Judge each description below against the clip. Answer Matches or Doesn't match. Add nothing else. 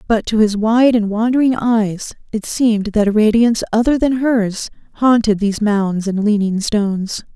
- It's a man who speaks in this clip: Doesn't match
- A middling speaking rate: Matches